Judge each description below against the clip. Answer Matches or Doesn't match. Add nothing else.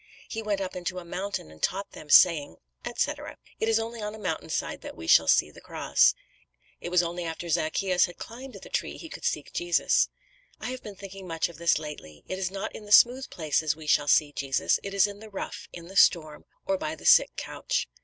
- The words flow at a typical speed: Doesn't match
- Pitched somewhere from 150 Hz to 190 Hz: Matches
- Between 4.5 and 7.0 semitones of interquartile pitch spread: Matches